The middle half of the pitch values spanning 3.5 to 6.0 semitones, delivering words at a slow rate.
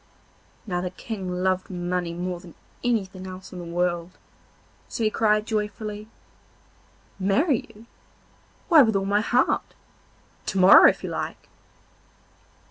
No: average, 3.1 semitones; slow, 130 wpm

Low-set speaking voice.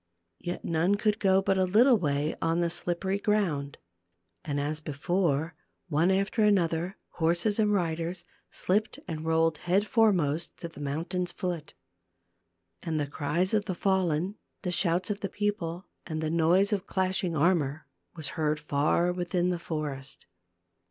No: medium, 175 Hz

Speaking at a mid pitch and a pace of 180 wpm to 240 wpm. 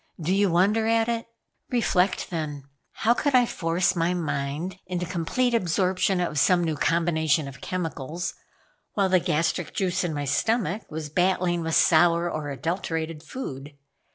No: medium, 175 Hz; average, 155 wpm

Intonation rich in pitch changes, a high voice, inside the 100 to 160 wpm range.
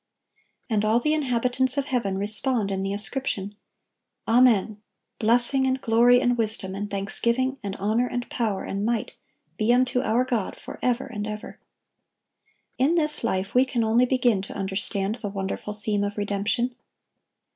No: average, 3.6 semitones; high, 230 Hz; average, 155 wpm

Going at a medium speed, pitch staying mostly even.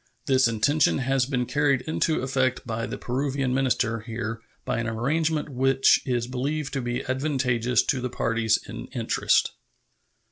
Yes: average, 150 wpm; narrow, 2.3 semitones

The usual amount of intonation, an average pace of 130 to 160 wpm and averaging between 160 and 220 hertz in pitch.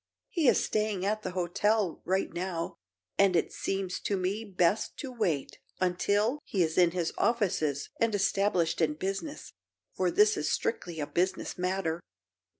Yes: average, 3.5 semitones; average, 155 wpm; high, 190 Hz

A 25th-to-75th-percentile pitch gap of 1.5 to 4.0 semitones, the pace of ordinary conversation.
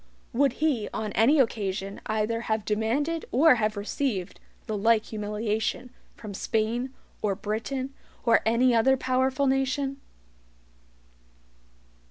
No: average, 3.7 semitones; slow, 115 wpm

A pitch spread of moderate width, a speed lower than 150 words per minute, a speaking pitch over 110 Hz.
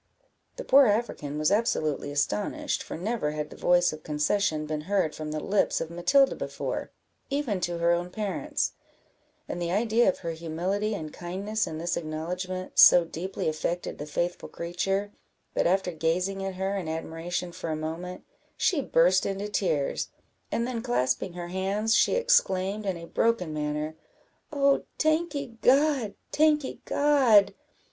No: average, 4.9 semitones; average, 155 wpm; medium, 185 Hz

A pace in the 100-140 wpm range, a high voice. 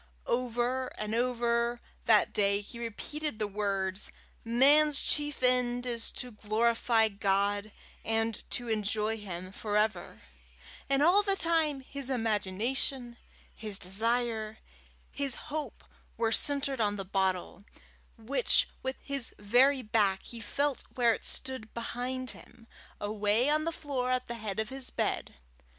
Yes: slow, 135 wpm; high, 235 Hz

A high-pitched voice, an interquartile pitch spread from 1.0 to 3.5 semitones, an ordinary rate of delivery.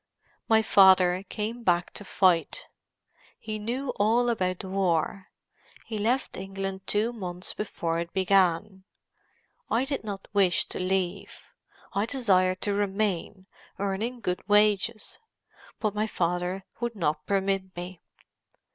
No: high, 195 Hz; narrow, 2.6 semitones; slow, 130 wpm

